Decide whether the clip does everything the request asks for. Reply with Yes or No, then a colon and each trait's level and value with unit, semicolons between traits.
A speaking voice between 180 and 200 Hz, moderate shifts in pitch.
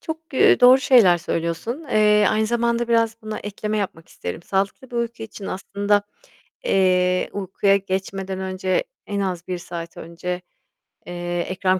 Yes: high, 195 Hz; average, 3.1 semitones